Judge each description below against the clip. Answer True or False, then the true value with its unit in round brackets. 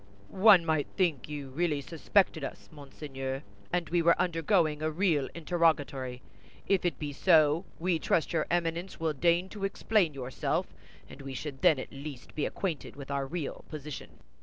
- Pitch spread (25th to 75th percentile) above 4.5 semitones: False (3.6 semitones)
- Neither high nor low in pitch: True (155 Hz)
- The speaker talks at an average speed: True (165 wpm)